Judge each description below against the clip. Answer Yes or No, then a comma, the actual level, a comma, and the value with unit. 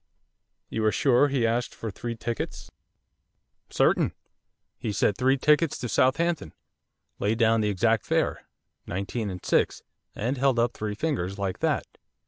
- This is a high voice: No, low, 115 Hz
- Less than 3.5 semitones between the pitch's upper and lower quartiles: No, average, 3.9 semitones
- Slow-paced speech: No, average, 145 wpm